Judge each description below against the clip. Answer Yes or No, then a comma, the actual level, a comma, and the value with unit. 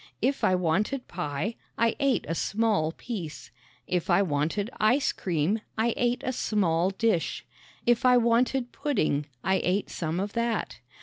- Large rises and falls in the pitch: Yes, wide, 5.7 semitones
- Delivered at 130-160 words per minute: Yes, average, 150 wpm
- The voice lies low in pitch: No, high, 210 Hz